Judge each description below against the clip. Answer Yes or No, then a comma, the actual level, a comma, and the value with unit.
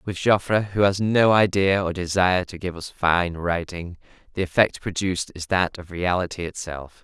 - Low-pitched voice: Yes, very low, 90 Hz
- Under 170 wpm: No, average, 180 wpm